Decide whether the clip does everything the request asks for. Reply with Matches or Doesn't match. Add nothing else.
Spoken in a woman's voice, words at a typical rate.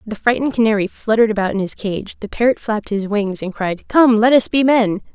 Doesn't match